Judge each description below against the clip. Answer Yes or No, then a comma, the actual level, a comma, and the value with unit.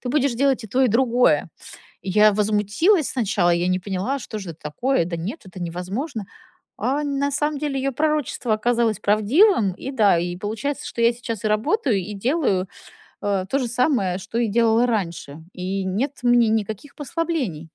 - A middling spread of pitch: No, wide, 5.8 semitones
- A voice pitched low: No, high, 225 Hz